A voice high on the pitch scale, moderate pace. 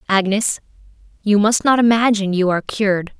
Yes: high, 205 Hz; average, 150 wpm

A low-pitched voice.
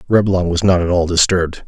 Yes: very low, 90 Hz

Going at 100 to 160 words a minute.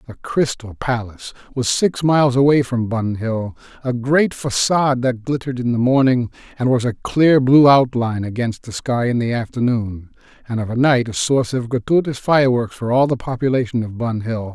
No: average, 190 wpm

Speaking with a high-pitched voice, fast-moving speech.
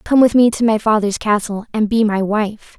Yes: high, 215 Hz; fast, 235 wpm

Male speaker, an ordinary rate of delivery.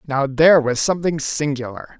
Yes: male; average, 150 wpm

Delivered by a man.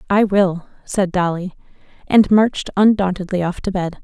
No: female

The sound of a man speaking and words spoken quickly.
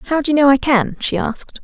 No: female; fast, 295 wpm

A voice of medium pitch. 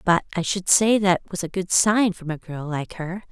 Yes: medium, 180 Hz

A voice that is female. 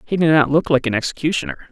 No: male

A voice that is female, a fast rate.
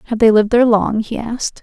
Yes: female; fast, 260 wpm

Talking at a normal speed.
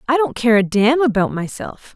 No: fast, 215 wpm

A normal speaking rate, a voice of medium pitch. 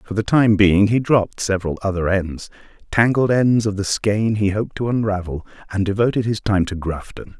No: average, 180 wpm; low, 105 Hz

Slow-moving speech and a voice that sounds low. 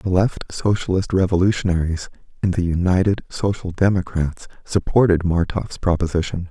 Yes: slow, 110 wpm; very low, 90 Hz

